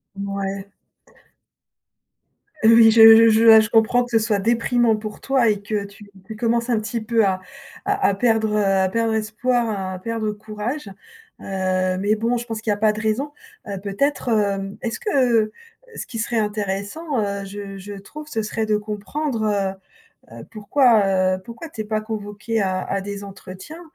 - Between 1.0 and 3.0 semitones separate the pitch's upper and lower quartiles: Yes, narrow, 2.5 semitones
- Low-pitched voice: No, high, 215 Hz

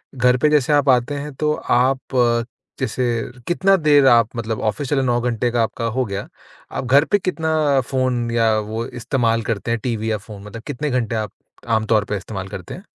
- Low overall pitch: Yes, low, 120 Hz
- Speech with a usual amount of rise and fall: Yes, average, 3.6 semitones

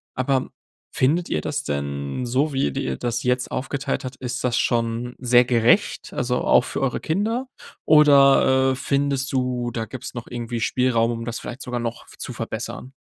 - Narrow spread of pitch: Yes, narrow, 2.3 semitones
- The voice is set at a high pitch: No, low, 125 Hz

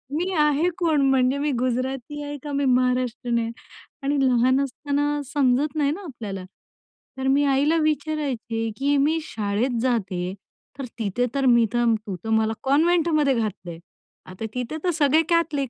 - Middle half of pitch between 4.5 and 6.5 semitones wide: No, average, 3.7 semitones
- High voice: Yes, very high, 270 Hz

